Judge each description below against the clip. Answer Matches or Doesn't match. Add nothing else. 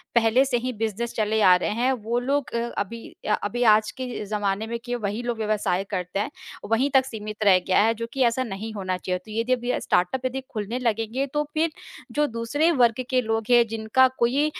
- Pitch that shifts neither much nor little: Matches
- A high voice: Matches